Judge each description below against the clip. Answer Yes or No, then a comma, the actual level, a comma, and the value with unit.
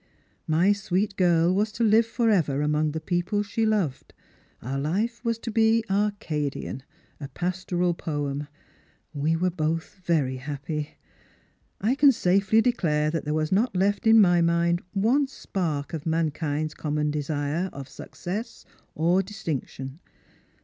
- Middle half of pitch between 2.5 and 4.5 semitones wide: No, average, 5.3 semitones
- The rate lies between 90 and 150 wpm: Yes, average, 145 wpm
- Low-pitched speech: No, medium, 175 Hz